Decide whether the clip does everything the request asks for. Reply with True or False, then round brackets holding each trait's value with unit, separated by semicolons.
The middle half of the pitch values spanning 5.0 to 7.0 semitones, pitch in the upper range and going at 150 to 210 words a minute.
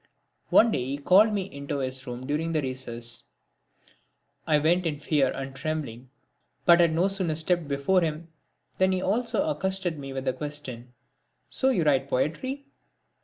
False (5.3 semitones; 155 Hz; 165 wpm)